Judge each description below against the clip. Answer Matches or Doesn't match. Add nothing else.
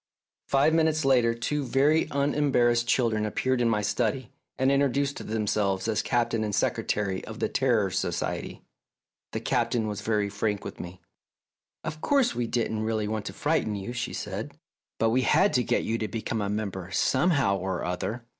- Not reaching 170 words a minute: Doesn't match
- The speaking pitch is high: Doesn't match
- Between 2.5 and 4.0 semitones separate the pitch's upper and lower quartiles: Doesn't match